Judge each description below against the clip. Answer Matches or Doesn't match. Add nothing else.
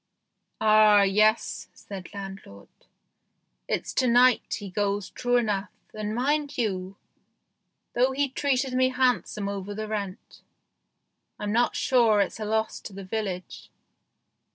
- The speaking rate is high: Doesn't match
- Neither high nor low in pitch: Doesn't match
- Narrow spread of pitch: Doesn't match